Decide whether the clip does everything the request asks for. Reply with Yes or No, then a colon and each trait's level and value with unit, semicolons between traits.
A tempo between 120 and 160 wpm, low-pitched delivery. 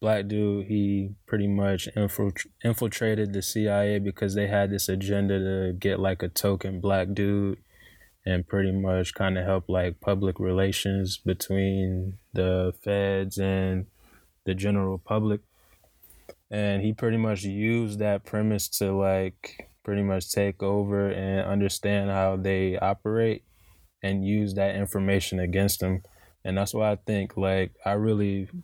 Yes: average, 140 wpm; low, 100 Hz